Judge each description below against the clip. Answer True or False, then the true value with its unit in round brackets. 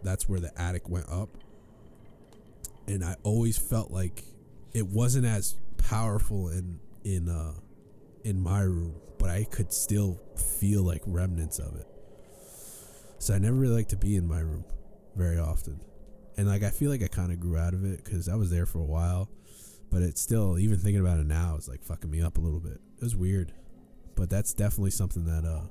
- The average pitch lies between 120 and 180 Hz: False (95 Hz)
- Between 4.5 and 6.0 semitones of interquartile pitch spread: False (3.5 semitones)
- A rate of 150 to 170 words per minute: False (200 wpm)